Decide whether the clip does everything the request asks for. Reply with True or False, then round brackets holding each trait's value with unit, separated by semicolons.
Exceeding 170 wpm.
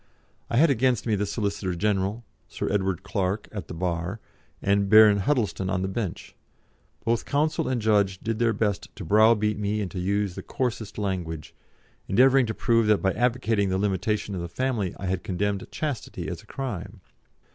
True (180 wpm)